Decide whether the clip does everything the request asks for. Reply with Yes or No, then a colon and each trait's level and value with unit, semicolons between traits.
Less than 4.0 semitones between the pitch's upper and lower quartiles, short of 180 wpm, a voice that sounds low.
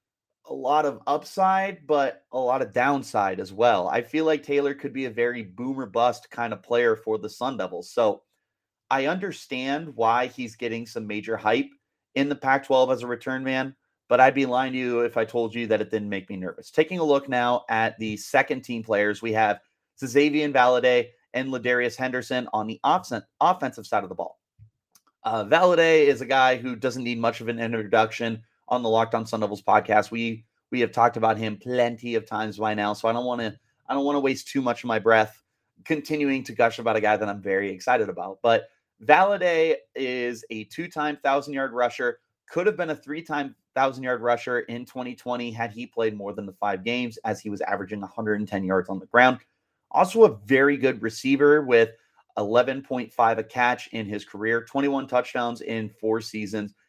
No: average, 3.3 semitones; fast, 205 wpm; low, 120 Hz